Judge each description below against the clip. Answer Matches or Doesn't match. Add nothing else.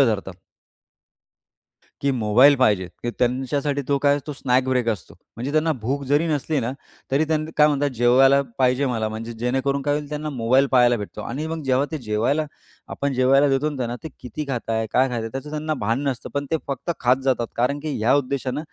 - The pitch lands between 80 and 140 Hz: Matches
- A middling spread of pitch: Matches